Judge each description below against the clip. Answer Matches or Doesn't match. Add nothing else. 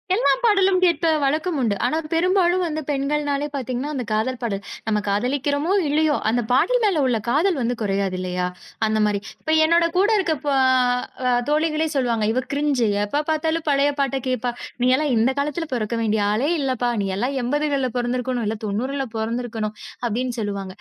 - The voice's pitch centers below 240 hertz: Doesn't match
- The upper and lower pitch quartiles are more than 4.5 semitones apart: Matches